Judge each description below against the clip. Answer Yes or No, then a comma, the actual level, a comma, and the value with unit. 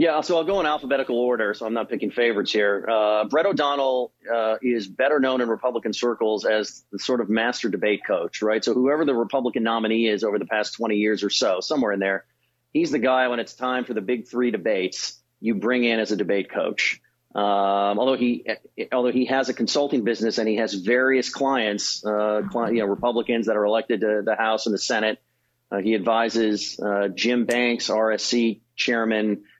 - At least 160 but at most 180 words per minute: No, fast, 205 wpm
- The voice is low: Yes, low, 115 Hz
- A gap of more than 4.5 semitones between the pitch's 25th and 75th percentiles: No, narrow, 2.6 semitones